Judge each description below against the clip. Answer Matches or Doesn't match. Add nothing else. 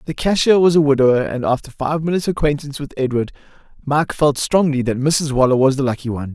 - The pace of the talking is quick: Matches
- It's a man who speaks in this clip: Matches